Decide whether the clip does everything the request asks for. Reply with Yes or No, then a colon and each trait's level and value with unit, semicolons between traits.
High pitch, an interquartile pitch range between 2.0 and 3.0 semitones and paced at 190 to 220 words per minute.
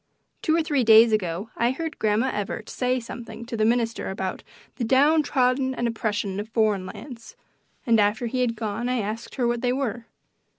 Yes: high, 235 Hz; average, 2.7 semitones; average, 195 wpm